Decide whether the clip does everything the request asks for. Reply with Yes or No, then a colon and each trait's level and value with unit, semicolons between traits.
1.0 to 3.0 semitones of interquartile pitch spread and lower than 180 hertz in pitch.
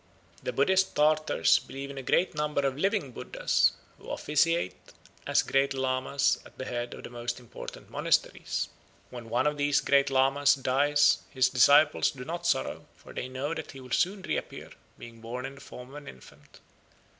Yes: narrow, 2.6 semitones; medium, 140 Hz